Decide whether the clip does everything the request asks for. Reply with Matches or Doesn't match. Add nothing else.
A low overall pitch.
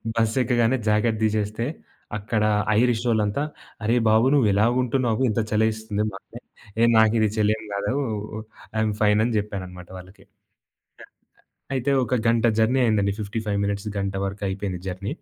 Matches